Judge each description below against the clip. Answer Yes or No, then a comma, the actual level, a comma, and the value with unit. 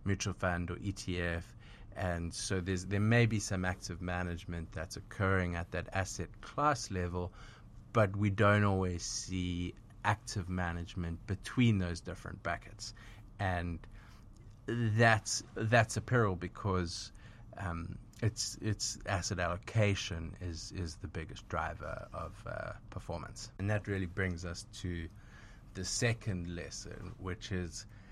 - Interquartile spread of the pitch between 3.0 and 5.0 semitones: Yes, average, 3.5 semitones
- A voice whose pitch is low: Yes, low, 100 Hz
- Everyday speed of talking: No, slow, 130 wpm